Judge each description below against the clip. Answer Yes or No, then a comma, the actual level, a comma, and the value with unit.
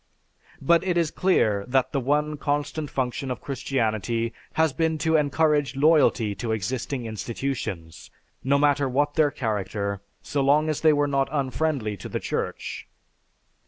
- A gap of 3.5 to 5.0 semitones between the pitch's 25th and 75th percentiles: Yes, average, 4.3 semitones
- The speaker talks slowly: No, average, 150 wpm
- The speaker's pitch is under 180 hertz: Yes, medium, 140 Hz